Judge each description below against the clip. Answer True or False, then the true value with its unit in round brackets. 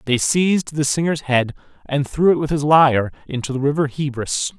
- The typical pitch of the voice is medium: True (145 Hz)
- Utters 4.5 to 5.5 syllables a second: True (5.3 syllables/s)